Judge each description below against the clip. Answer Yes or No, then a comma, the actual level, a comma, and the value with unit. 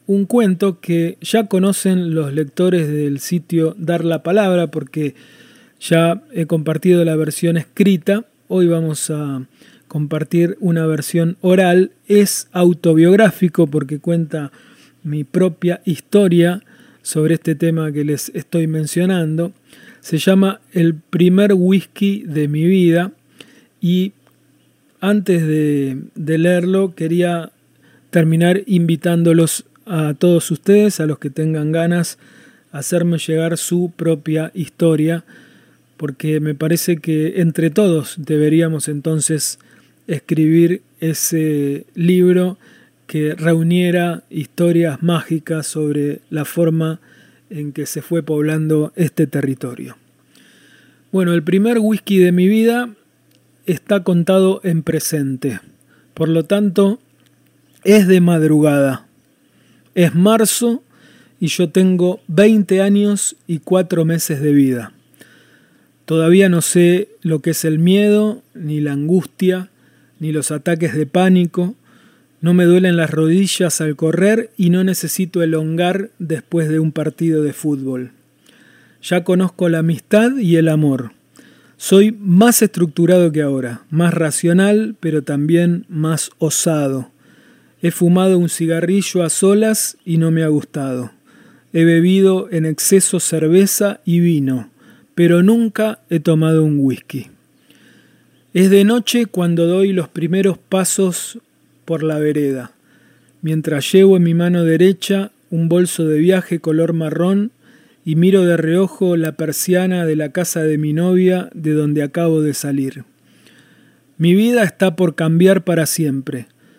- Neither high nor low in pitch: Yes, medium, 170 Hz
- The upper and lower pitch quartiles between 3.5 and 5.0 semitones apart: No, average, 3.1 semitones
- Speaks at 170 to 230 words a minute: No, slow, 125 wpm